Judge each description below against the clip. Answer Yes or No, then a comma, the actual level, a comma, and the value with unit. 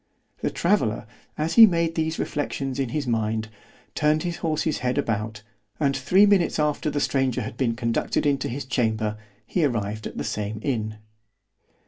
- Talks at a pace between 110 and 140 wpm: No, average, 165 wpm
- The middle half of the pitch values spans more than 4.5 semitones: Yes, wide, 5.5 semitones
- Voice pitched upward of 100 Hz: Yes, low, 135 Hz